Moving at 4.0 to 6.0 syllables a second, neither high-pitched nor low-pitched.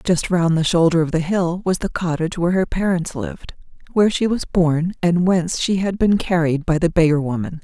Yes: 5.5 syllables/s; medium, 175 Hz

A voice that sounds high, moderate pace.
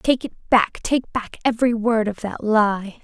Yes: high, 225 Hz; average, 180 wpm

